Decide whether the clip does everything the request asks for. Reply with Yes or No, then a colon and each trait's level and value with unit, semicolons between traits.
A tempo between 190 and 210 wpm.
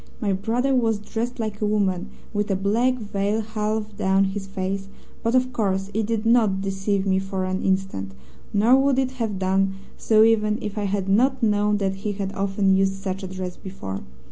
Yes: average, 195 wpm